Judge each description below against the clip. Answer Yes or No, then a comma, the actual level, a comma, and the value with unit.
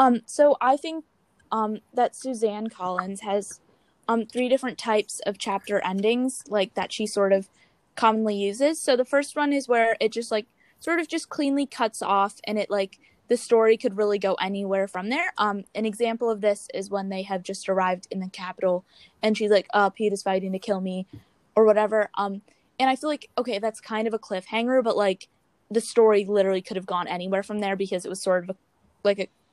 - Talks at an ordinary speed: No, fast, 215 wpm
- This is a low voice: No, high, 210 Hz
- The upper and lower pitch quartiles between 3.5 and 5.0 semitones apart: No, average, 3.1 semitones